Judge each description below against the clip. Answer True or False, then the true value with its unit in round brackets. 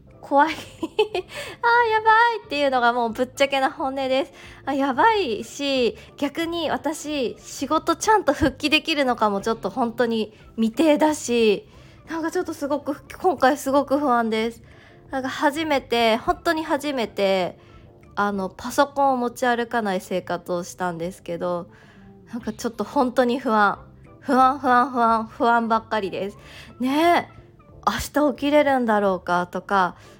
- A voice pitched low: False (260 Hz)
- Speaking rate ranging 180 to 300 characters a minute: True (280 characters per minute)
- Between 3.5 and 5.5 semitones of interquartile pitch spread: True (5.2 semitones)